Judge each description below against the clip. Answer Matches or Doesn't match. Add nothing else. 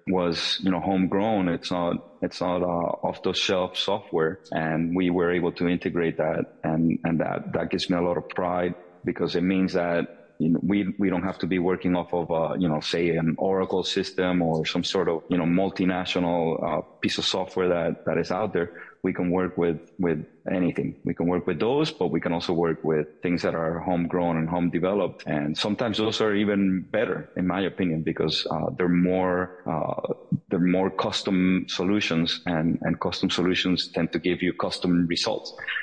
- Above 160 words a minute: Matches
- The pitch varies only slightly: Matches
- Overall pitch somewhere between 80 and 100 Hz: Matches